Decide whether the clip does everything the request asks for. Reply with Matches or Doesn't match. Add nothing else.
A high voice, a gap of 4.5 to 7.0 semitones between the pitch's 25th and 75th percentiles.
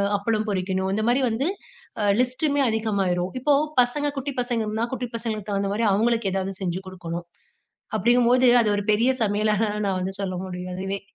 Doesn't match